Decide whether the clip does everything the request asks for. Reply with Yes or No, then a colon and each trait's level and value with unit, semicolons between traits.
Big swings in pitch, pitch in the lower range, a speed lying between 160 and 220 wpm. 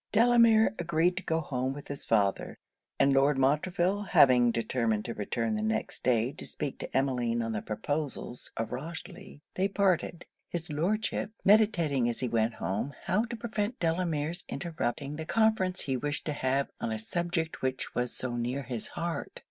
No: wide, 6.5 semitones; medium, 145 Hz; average, 170 wpm